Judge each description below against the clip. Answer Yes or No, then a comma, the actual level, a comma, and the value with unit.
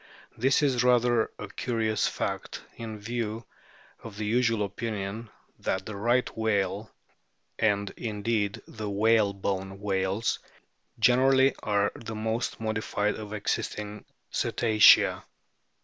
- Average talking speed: No, slow, 110 wpm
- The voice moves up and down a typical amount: No, narrow, 2.2 semitones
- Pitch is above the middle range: No, low, 110 Hz